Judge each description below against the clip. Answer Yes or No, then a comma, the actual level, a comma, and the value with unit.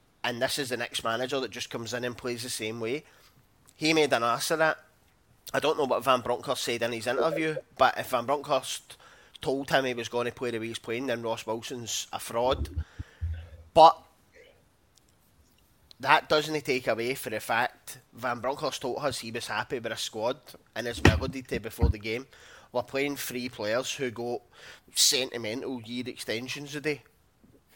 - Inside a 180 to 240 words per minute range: Yes, average, 185 wpm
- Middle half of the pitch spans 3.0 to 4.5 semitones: No, narrow, 2.6 semitones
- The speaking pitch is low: Yes, low, 120 Hz